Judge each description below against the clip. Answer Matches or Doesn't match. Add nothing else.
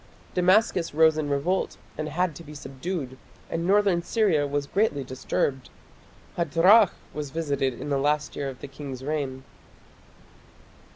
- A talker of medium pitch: Matches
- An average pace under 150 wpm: Matches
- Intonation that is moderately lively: Matches